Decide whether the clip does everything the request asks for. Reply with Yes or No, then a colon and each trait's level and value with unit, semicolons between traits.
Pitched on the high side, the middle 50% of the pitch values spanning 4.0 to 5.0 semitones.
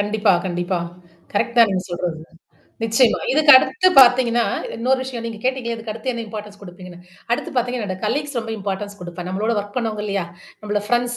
No: high, 220 Hz; average, 3.5 semitones